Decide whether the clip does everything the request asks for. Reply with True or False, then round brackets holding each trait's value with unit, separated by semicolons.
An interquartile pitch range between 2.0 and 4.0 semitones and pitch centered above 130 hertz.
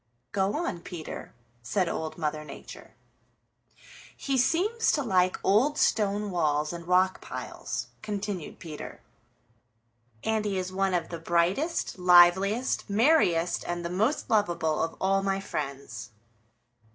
True (3.7 semitones; 185 Hz)